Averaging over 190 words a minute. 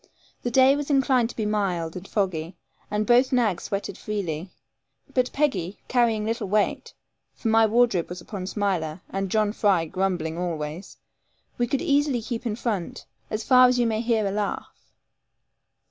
No: average, 165 wpm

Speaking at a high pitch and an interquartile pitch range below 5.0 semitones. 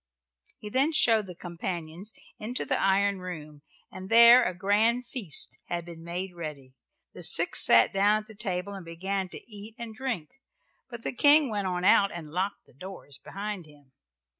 Yes: high, 195 Hz; average, 4.1 semitones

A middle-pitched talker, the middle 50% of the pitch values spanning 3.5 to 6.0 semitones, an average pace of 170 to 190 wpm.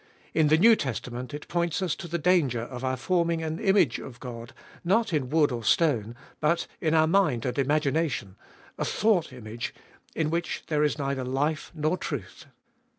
Yes: medium, 150 Hz; average, 4.8 semitones; average, 180 wpm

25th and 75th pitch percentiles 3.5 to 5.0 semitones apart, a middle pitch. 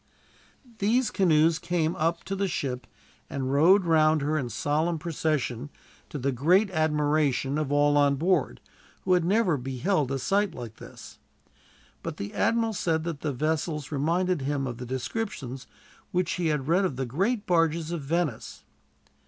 Yes: average, 4.3 semitones; medium, 155 Hz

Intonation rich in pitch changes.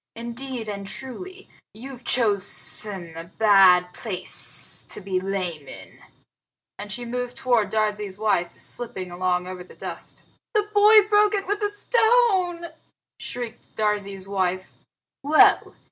Yes: wide, 6.4 semitones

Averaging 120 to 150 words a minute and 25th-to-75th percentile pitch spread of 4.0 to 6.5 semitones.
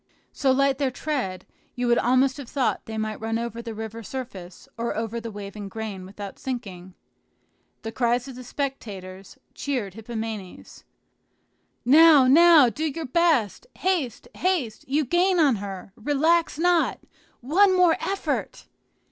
Yes: average, 145 wpm; average, 5.2 semitones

